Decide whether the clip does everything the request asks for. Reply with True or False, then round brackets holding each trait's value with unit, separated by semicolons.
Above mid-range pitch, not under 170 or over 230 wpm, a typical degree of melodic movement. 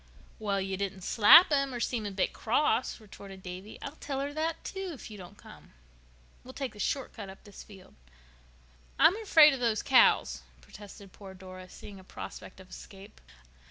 False (210 Hz; 185 wpm; 6.0 semitones)